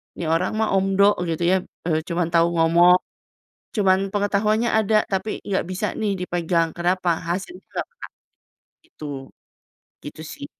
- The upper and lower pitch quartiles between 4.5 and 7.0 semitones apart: No, average, 3.3 semitones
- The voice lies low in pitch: No, medium, 185 Hz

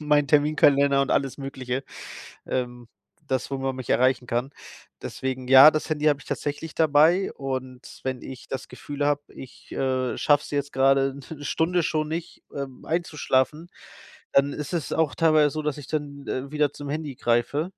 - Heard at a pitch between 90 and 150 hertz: Yes, medium, 140 Hz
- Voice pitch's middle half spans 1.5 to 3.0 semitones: Yes, narrow, 2.4 semitones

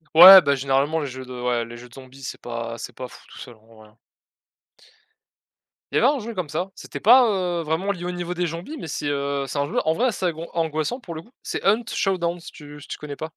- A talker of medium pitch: Yes, medium, 155 Hz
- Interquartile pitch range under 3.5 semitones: No, average, 5.0 semitones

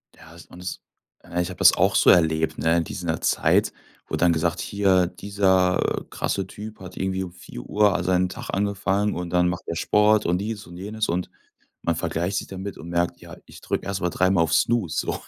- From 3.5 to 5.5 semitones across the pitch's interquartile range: No, narrow, 2.4 semitones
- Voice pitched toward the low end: Yes, very low, 90 Hz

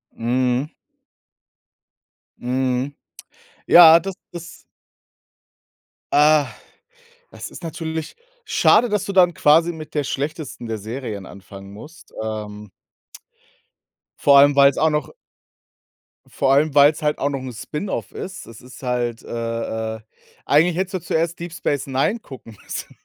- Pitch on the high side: No, medium, 140 Hz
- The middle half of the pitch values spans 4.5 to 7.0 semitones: Yes, average, 5.0 semitones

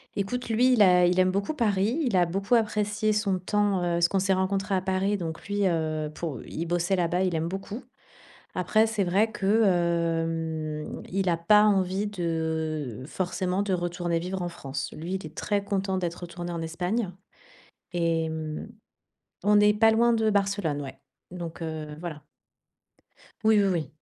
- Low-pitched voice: No, medium, 185 Hz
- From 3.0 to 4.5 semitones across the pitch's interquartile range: Yes, average, 3.4 semitones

